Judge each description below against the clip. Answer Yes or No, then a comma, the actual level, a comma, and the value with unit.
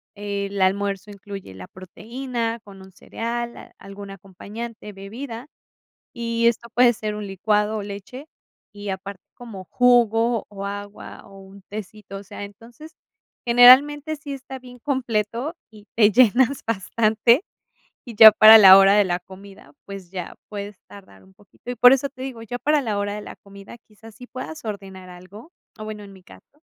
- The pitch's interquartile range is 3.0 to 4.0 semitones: Yes, average, 3.3 semitones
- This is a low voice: No, high, 210 Hz